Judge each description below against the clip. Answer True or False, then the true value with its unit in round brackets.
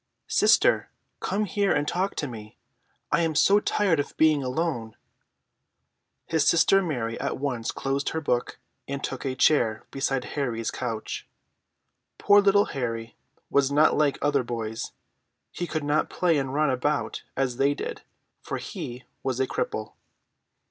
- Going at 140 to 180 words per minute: True (150 wpm)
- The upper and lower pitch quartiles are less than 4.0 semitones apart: False (4.5 semitones)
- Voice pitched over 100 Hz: True (140 Hz)